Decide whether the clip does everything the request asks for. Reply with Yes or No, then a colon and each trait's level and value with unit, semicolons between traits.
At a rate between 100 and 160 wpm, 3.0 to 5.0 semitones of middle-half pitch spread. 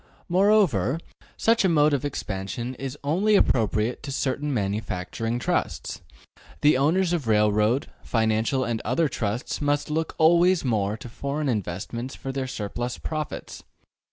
No: slow, 135 wpm; wide, 5.5 semitones